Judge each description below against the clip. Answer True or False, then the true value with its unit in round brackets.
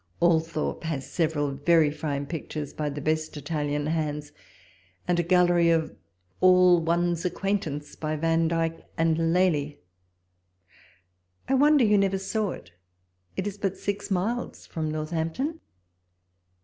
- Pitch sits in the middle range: True (165 Hz)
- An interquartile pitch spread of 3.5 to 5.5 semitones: False (3.0 semitones)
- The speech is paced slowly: True (125 wpm)